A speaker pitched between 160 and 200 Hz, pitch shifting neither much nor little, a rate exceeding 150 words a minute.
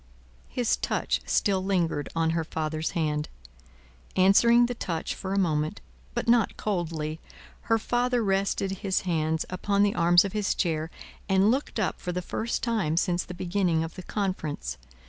Yes: medium, 185 Hz; average, 3.9 semitones; average, 165 wpm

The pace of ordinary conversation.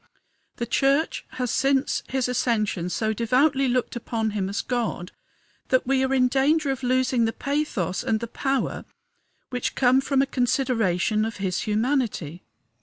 Yes: average, 155 wpm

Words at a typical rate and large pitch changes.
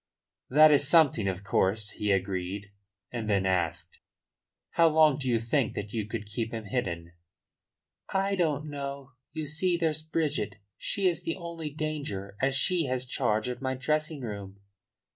Yes: average, 160 wpm; wide, 6.9 semitones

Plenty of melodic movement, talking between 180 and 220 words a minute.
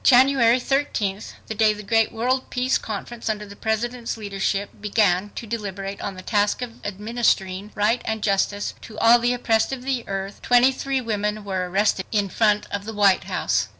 No: average, 2.9 semitones; average, 185 wpm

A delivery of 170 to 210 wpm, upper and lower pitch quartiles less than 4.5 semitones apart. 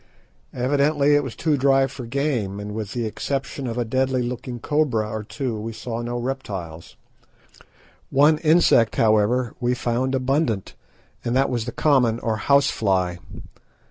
No: average, 155 wpm; average, 3.7 semitones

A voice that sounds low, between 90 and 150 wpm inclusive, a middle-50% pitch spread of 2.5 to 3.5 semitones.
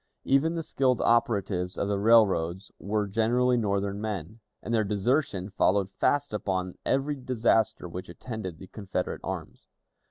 No: low, 105 Hz; average, 140 wpm; average, 4.0 semitones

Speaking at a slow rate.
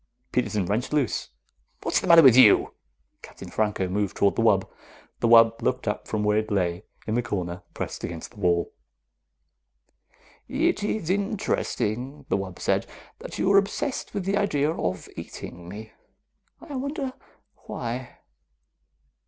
No: average, 150 wpm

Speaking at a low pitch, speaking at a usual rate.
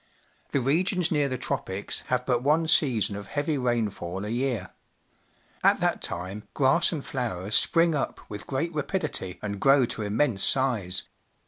Yes: low, 125 Hz; average, 160 wpm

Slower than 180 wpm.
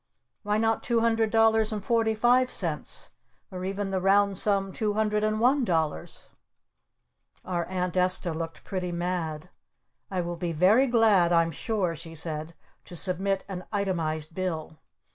Yes: average, 155 wpm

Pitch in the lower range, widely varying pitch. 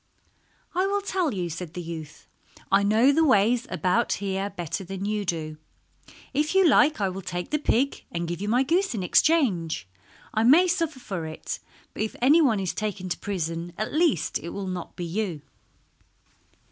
No: high, 200 Hz; wide, 8.1 semitones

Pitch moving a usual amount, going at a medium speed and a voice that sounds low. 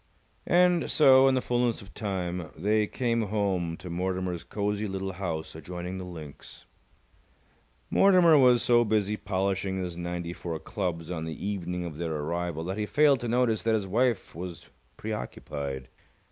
Yes: average, 4.5 semitones; average, 160 wpm; very low, 95 Hz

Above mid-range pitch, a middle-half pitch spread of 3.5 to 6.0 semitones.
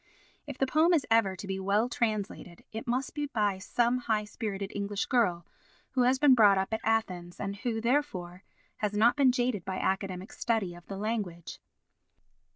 Yes: high, 215 Hz; average, 4.0 semitones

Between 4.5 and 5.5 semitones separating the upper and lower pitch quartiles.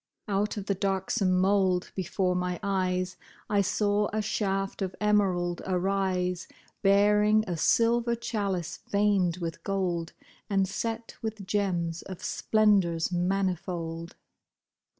No: narrow, 2.4 semitones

